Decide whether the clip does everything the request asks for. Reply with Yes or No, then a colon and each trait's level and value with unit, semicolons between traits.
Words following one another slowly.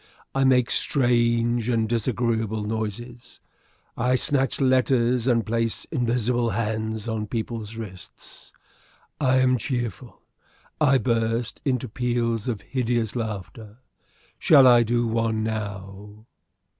Yes: slow, 110 wpm